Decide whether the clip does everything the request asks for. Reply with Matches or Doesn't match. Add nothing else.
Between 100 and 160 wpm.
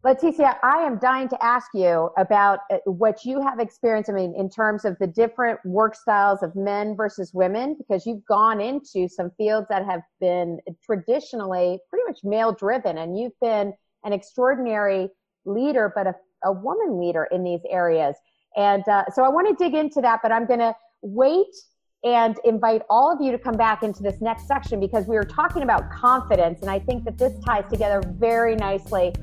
Doesn't match